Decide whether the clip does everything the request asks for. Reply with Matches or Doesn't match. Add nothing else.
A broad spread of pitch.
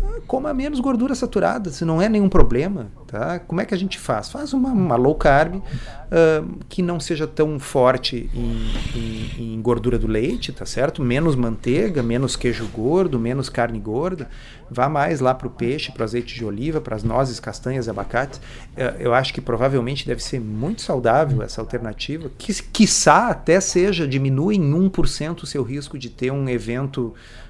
Matches